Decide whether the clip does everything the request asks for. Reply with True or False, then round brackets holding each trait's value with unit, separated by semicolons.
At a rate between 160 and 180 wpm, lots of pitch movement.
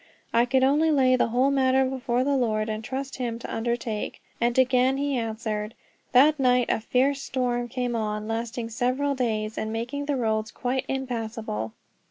False (175 wpm; 2.7 semitones)